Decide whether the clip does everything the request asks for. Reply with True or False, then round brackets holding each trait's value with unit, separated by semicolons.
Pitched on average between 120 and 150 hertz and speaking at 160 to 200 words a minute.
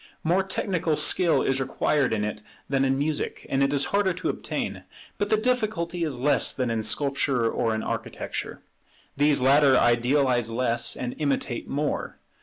True (140 Hz; 165 wpm)